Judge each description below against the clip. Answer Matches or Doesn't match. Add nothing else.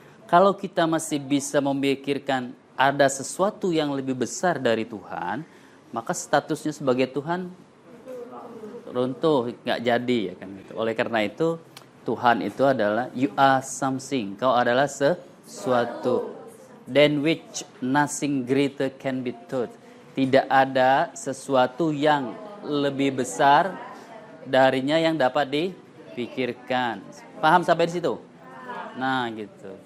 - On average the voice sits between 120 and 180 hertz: Matches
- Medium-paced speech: Matches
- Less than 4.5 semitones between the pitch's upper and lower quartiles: Matches